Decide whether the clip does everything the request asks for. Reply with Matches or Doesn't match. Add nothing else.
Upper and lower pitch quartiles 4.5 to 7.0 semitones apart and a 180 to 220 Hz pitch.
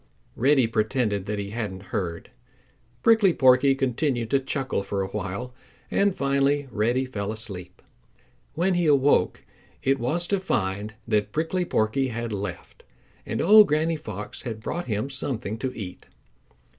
Doesn't match